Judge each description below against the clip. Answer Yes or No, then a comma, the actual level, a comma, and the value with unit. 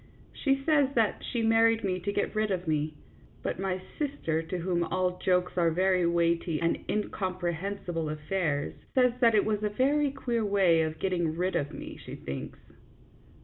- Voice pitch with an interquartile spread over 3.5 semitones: Yes, average, 4.4 semitones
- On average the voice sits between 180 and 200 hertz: Yes, medium, 185 Hz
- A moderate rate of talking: Yes, average, 180 wpm